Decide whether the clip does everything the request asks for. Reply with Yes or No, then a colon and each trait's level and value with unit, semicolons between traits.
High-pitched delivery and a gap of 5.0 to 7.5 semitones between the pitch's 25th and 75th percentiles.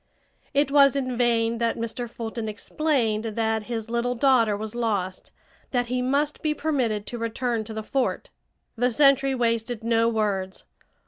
No: high, 235 Hz; narrow, 2.5 semitones